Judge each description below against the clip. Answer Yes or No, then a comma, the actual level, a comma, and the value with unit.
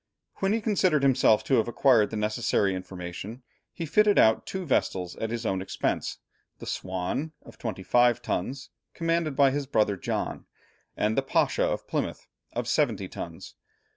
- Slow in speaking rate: No, average, 165 wpm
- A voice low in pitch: Yes, low, 120 Hz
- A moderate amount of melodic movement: No, wide, 6.4 semitones